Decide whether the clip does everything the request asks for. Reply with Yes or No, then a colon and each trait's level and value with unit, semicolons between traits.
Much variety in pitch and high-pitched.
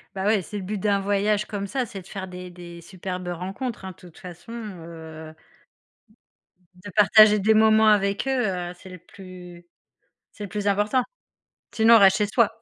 No: average, 2.8 semitones; high, 195 Hz